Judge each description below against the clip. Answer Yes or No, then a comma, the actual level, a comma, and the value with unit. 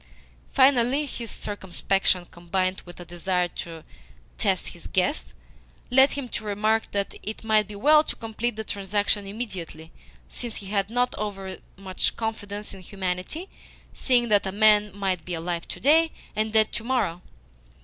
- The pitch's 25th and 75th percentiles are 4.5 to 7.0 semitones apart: No, average, 3.5 semitones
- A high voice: Yes, high, 205 Hz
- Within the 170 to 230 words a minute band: No, average, 155 wpm